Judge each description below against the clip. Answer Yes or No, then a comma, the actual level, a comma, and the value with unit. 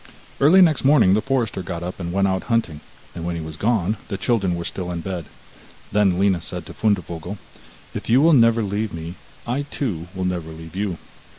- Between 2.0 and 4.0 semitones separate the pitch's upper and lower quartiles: No, average, 4.9 semitones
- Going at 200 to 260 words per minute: Yes, fast, 205 wpm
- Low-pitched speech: Yes, very low, 95 Hz